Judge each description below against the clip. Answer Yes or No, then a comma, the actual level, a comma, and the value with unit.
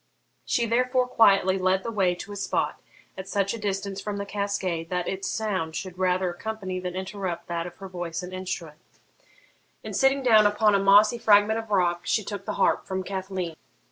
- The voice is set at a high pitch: Yes, high, 195 Hz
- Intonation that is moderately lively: No, narrow, 2.3 semitones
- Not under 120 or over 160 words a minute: No, average, 195 wpm